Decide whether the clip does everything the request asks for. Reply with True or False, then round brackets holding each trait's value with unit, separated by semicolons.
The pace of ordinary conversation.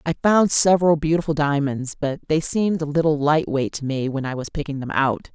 False (225 wpm)